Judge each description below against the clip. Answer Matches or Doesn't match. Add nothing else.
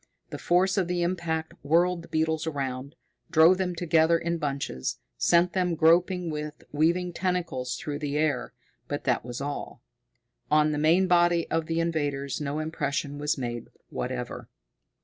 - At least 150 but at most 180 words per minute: Matches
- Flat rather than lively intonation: Doesn't match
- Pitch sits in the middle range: Matches